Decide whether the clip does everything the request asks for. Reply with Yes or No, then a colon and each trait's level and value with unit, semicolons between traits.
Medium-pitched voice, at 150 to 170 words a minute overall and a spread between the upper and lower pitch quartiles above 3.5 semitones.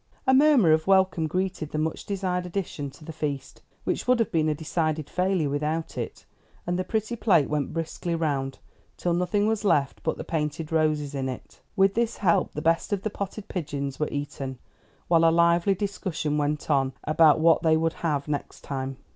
No: medium, 160 Hz; average, 195 wpm; average, 3.9 semitones